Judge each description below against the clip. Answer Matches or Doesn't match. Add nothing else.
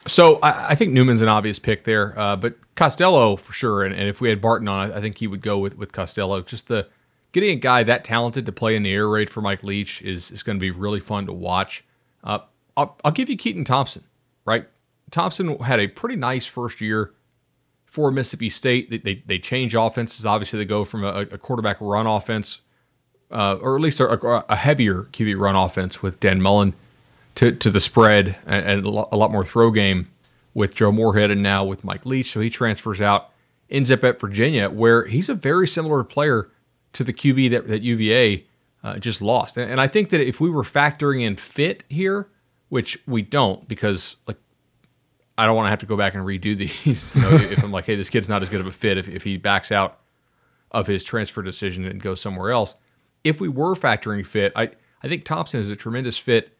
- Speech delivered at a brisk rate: Matches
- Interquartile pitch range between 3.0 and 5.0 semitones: Matches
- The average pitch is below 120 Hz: Matches